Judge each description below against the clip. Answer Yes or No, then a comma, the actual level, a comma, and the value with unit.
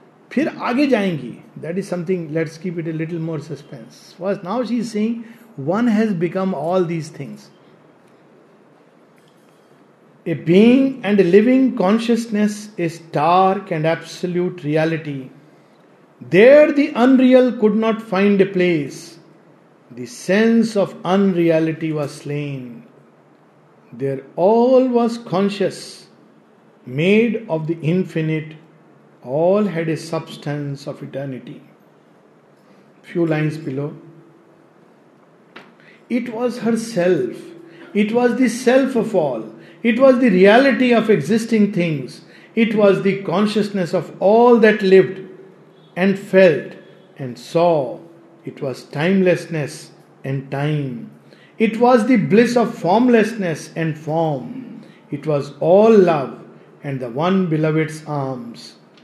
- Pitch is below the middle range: No, medium, 180 Hz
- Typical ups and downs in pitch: No, wide, 5.7 semitones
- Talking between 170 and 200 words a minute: No, average, 115 wpm